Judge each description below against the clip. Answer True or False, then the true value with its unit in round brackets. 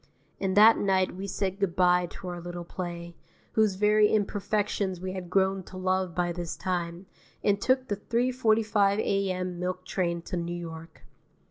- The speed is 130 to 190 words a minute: True (165 wpm)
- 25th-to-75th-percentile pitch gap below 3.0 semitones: True (2.5 semitones)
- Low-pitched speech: False (185 Hz)